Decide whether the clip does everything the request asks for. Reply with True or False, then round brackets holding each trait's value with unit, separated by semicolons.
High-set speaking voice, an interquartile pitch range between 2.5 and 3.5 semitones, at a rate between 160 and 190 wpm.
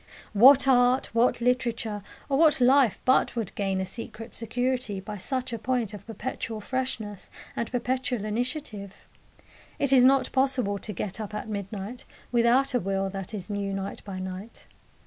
False (230 Hz; 4.0 semitones; 165 wpm)